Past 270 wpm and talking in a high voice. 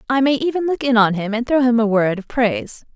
Yes: fast, 285 wpm; high, 235 Hz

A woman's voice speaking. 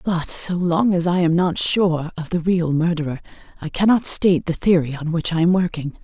Yes: female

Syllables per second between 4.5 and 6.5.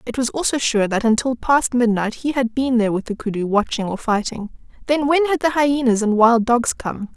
Yes: 5.3 syllables/s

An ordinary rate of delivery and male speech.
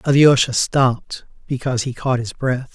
Yes: average, 155 wpm; male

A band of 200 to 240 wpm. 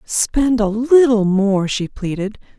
No: average, 140 wpm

